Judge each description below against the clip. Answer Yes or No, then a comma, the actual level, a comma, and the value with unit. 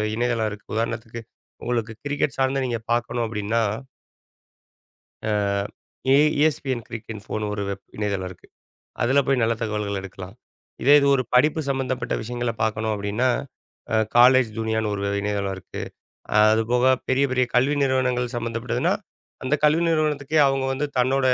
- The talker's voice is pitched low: Yes, low, 120 Hz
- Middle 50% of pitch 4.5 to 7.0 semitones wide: No, average, 3.5 semitones